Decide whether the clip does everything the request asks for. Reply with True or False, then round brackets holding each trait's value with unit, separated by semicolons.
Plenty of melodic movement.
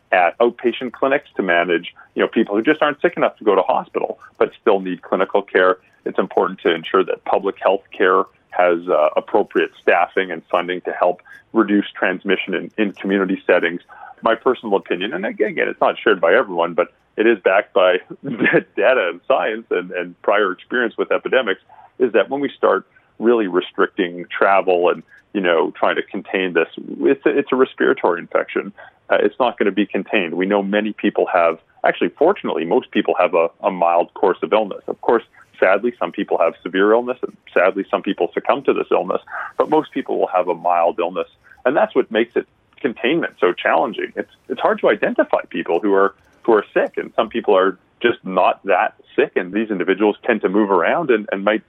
True (6.6 semitones)